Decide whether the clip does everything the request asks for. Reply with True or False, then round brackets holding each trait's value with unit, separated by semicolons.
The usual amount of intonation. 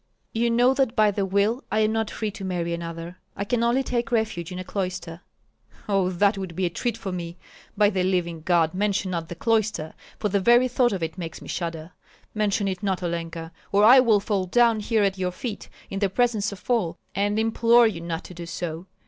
True (4.1 semitones)